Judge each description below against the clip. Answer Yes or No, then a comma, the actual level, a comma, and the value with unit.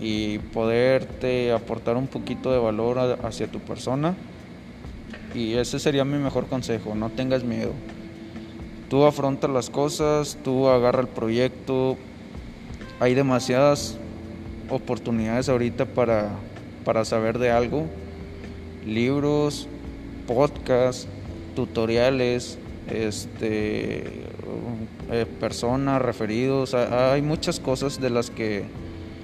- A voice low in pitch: Yes, low, 120 Hz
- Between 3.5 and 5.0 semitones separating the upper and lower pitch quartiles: No, average, 2.8 semitones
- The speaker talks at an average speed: No, slow, 100 wpm